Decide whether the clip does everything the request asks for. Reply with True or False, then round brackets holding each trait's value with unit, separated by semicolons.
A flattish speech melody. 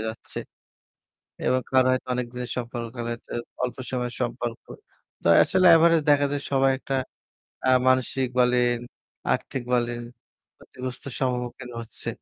True (1.4 semitones)